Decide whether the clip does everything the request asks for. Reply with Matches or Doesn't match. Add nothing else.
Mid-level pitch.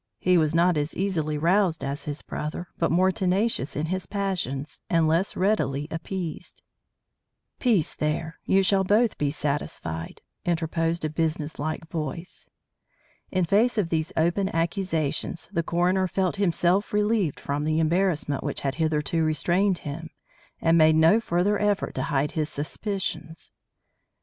Matches